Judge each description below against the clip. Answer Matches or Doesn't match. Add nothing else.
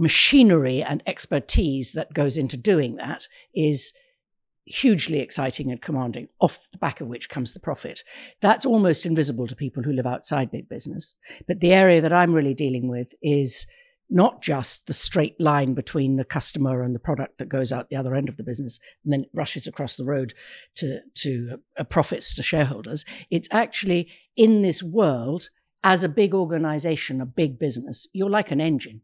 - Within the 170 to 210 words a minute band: Matches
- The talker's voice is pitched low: Doesn't match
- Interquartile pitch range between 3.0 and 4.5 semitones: Doesn't match